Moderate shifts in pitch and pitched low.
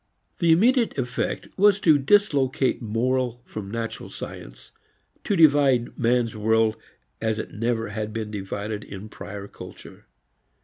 Yes: average, 4.5 semitones; low, 115 Hz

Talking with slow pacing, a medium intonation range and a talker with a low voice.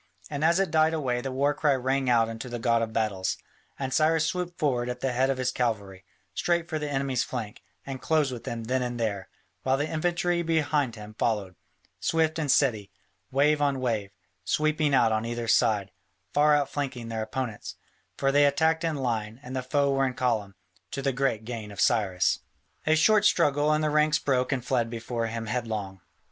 No: average, 200 wpm; average, 4.5 semitones; low, 130 Hz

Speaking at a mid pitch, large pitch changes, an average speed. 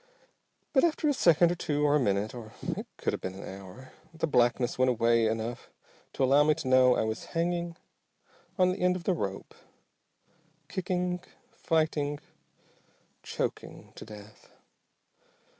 Yes: medium, 145 Hz; wide, 6.9 semitones; average, 155 wpm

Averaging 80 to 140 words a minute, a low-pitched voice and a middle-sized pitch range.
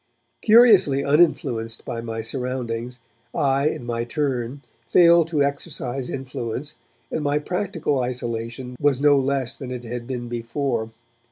Yes: slow, 135 wpm; low, 130 Hz; average, 3.4 semitones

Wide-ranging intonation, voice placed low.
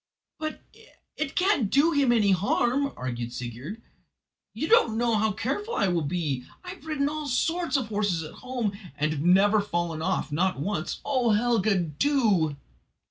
No: wide, 8.4 semitones; high, 210 Hz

